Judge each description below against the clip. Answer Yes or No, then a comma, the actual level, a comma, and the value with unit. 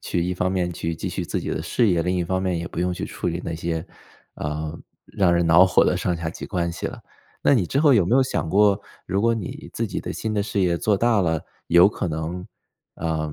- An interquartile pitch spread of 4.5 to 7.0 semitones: No, average, 3.1 semitones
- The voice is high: No, very low, 90 Hz